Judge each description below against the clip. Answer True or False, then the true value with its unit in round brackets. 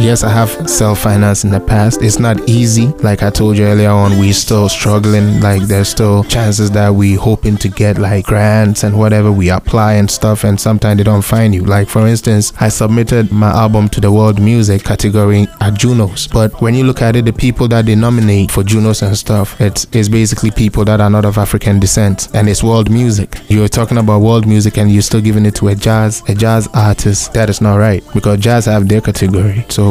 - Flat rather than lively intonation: True (1.5 semitones)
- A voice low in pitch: True (105 Hz)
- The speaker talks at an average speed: False (225 wpm)